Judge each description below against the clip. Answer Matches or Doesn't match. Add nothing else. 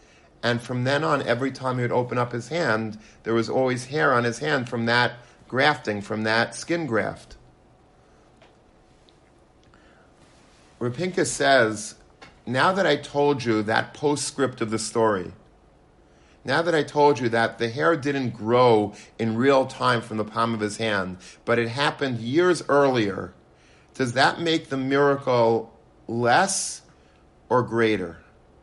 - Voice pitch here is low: Matches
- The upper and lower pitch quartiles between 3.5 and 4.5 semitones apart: Matches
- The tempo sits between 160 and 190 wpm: Doesn't match